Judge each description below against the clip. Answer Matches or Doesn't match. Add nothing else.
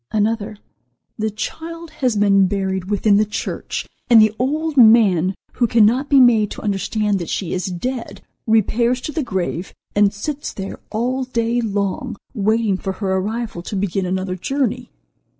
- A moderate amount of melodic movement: Matches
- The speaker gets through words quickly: Doesn't match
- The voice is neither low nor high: Doesn't match